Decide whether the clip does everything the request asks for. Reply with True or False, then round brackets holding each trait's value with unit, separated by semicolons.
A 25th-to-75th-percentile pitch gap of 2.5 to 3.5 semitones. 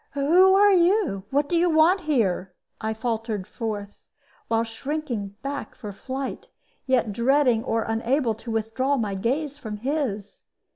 False (5.1 semitones)